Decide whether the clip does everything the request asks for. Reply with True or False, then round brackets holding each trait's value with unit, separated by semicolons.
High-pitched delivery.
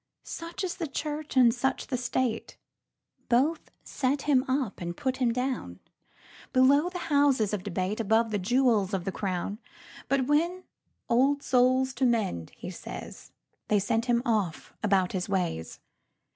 True (245 Hz)